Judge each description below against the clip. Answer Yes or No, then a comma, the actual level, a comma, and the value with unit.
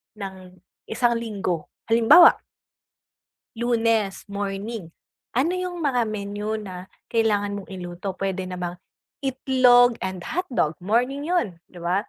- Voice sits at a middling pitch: No, high, 210 Hz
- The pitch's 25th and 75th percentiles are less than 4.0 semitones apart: No, average, 4.4 semitones